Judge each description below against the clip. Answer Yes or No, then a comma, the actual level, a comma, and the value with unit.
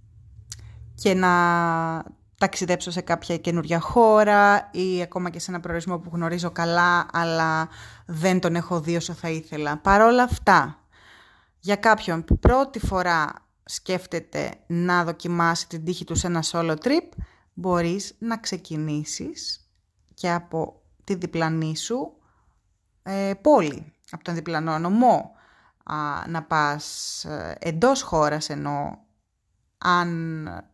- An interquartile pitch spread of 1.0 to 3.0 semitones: Yes, narrow, 2.4 semitones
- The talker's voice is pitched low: No, medium, 170 Hz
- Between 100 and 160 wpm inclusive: Yes, slow, 115 wpm